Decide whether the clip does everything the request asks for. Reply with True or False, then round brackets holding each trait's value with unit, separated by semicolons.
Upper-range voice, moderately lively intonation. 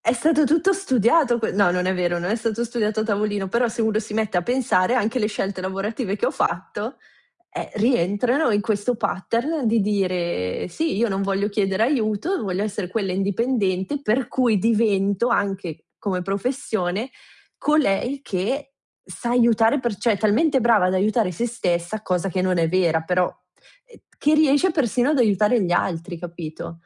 True (215 Hz; 4.4 semitones)